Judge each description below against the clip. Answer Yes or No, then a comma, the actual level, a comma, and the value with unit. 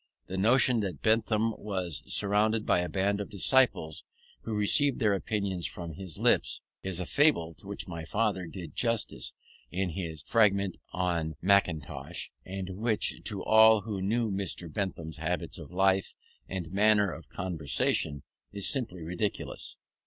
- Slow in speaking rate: No, average, 150 wpm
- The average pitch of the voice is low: Yes, very low, 95 Hz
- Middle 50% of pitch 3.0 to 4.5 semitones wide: Yes, average, 3.5 semitones